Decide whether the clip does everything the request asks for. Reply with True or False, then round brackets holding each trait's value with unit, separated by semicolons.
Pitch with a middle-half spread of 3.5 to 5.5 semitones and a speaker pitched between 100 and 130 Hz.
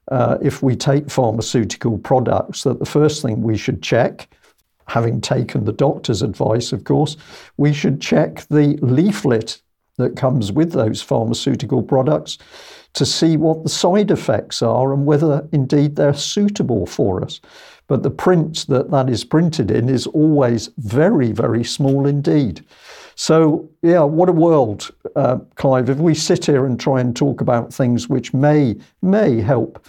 False (3.8 semitones; 140 Hz)